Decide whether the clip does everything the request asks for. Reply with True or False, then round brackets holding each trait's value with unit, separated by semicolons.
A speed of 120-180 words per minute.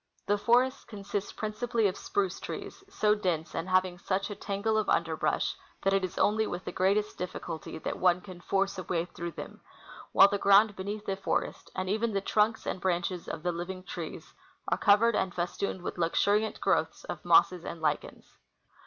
False (195 wpm)